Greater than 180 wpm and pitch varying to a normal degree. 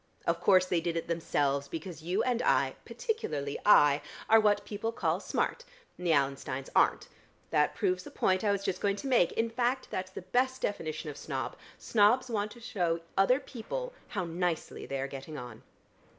No: average, 190 wpm; wide, 6.2 semitones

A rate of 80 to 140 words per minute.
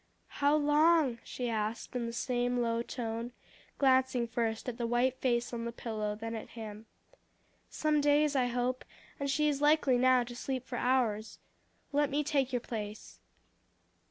No: average, 165 wpm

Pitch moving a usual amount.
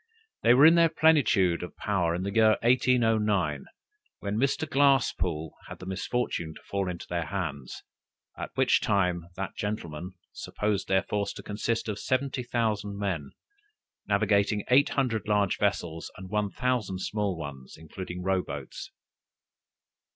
Yes: average, 4.2 semitones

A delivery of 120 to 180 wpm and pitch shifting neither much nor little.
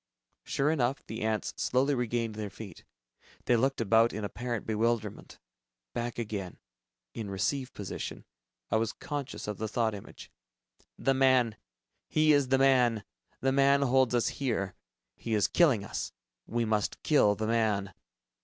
Yes: average, 150 wpm; average, 3.6 semitones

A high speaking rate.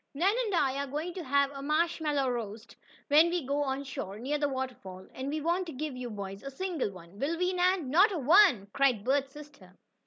Yes: fast, 215 wpm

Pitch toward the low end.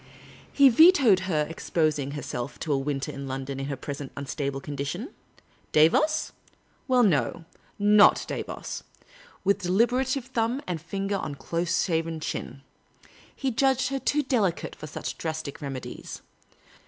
No: medium, 170 Hz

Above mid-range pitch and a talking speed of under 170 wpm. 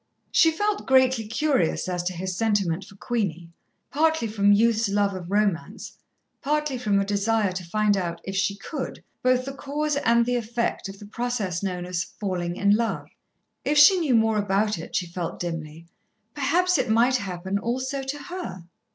No: high, 215 Hz; average, 175 wpm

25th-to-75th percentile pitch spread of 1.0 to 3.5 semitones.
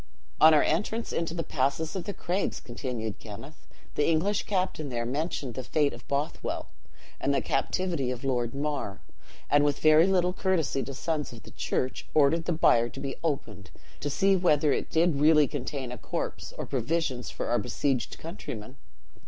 No: average, 4.3 semitones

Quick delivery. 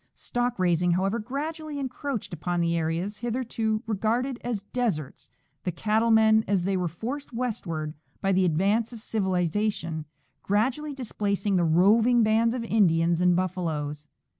No: average, 140 wpm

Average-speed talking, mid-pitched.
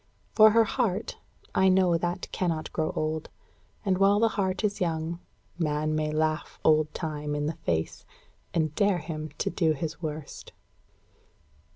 Yes: average, 155 wpm; medium, 160 Hz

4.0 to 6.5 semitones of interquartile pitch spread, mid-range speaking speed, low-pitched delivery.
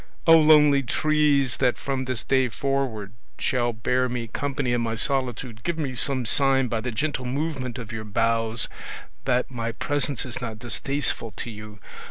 No: average, 3.2 semitones; average, 170 wpm; low, 125 Hz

